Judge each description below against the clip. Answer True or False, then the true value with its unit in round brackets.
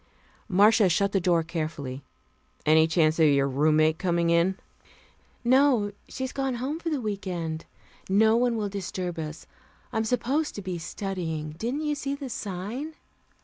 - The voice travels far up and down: True (6.8 semitones)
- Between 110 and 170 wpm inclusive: True (155 wpm)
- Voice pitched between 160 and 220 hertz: True (190 Hz)